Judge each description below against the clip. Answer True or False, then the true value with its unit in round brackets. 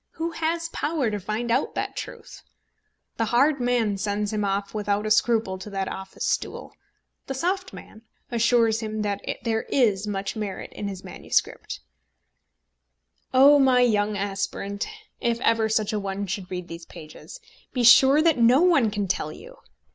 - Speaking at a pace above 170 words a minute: False (165 wpm)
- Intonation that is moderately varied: True (3.8 semitones)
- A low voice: False (220 Hz)